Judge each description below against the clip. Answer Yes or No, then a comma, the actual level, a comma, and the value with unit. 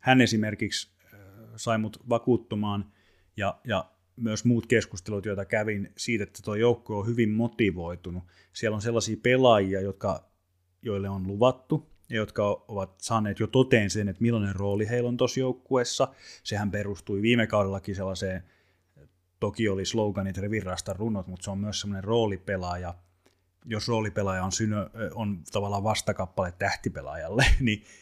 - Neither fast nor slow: Yes, average, 140 wpm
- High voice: No, low, 105 Hz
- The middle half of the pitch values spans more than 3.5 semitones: No, average, 2.8 semitones